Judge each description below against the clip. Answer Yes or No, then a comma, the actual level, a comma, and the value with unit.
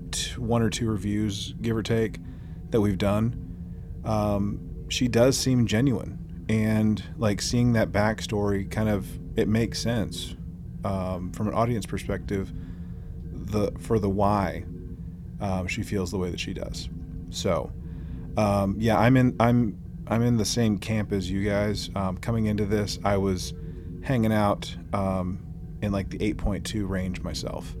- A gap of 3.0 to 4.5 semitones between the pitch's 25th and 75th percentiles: Yes, average, 3.7 semitones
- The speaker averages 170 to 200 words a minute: No, average, 155 wpm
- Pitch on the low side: Yes, low, 100 Hz